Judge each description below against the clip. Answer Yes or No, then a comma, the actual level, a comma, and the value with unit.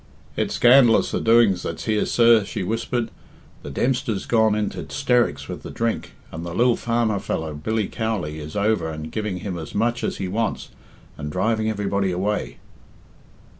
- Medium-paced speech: Yes, average, 170 wpm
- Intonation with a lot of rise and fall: No, average, 4.3 semitones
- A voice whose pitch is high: No, low, 105 Hz